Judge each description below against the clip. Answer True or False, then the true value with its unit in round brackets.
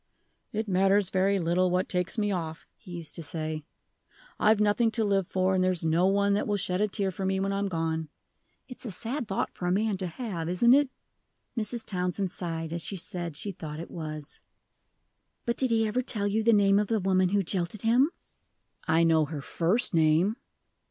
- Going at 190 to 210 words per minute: True (205 wpm)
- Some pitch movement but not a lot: True (3.7 semitones)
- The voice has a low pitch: False (190 Hz)